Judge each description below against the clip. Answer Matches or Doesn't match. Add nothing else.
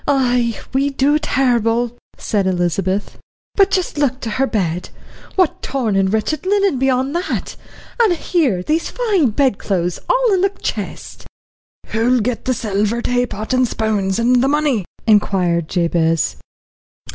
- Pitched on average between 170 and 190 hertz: Doesn't match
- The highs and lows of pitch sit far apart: Matches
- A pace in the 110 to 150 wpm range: Matches